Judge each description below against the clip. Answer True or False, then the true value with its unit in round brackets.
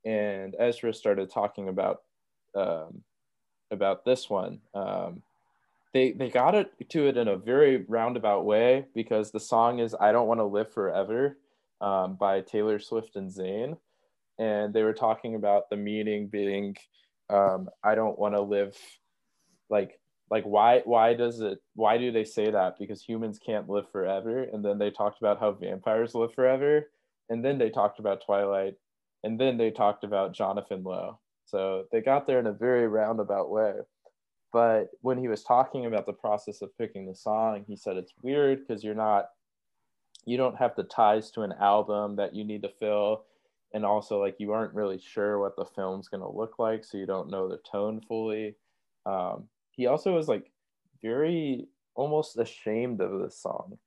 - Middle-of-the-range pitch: False (105 Hz)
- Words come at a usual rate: True (180 wpm)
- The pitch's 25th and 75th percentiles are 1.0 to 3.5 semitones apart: True (2.4 semitones)